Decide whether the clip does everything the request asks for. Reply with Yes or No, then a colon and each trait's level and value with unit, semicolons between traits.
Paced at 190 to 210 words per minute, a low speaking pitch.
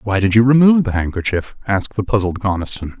Yes: average, 200 wpm; low, 105 Hz